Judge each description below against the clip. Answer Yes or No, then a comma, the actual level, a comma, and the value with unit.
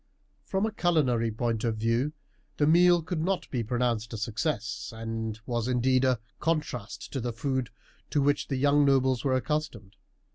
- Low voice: Yes, low, 130 Hz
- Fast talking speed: No, average, 170 wpm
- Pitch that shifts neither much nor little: Yes, average, 4.6 semitones